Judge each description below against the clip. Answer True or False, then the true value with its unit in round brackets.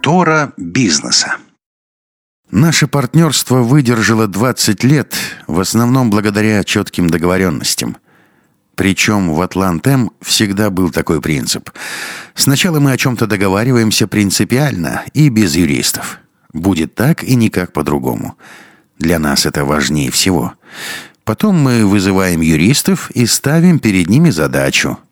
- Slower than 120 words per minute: True (110 wpm)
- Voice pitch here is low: True (110 Hz)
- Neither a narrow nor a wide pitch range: False (6.5 semitones)